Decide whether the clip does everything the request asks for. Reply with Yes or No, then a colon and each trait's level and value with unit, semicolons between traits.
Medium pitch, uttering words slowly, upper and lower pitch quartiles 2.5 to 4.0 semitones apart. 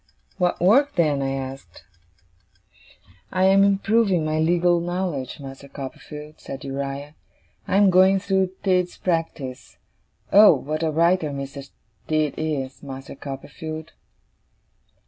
No: medium, 155 Hz; slow, 120 wpm; average, 5.0 semitones